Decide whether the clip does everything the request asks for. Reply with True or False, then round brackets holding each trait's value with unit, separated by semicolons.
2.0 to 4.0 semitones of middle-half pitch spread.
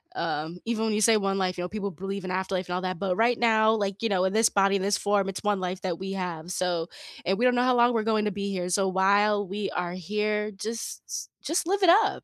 True (2.8 semitones)